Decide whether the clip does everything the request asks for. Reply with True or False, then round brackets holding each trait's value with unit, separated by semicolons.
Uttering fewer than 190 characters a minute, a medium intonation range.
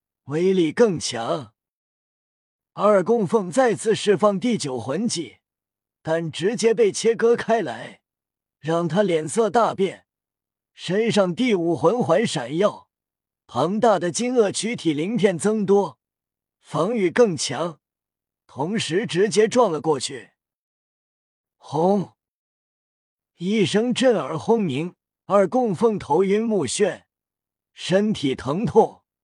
False (160 characters per minute; 6.0 semitones)